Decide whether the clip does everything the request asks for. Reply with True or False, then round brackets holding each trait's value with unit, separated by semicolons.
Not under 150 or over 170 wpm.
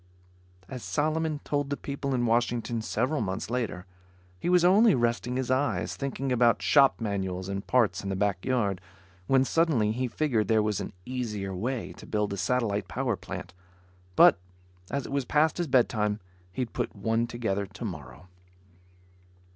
True (165 wpm)